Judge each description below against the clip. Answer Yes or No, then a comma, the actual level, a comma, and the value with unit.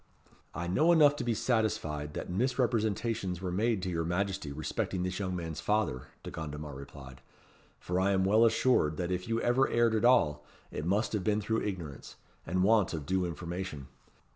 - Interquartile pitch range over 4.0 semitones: Yes, average, 5.2 semitones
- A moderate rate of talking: Yes, average, 185 wpm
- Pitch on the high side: No, very low, 95 Hz